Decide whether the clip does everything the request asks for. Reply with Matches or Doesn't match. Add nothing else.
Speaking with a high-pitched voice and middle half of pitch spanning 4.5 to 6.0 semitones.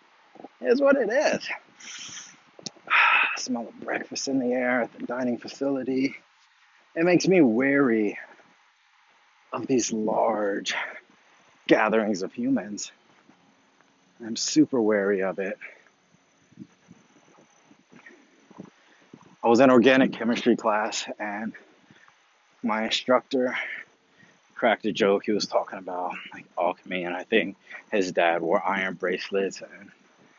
Doesn't match